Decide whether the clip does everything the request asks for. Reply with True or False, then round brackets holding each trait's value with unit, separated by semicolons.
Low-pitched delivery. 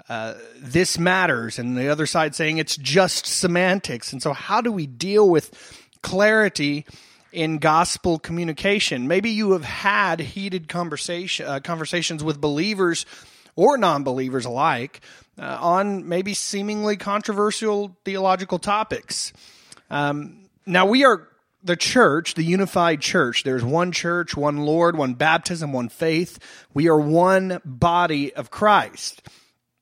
False (170 Hz)